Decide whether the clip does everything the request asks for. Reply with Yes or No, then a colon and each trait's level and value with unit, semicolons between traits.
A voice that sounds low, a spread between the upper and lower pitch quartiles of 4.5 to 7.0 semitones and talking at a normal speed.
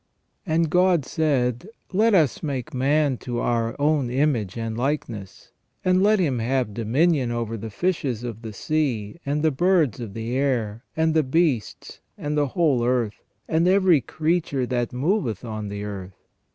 Yes: low, 130 Hz; wide, 5.4 semitones; average, 165 wpm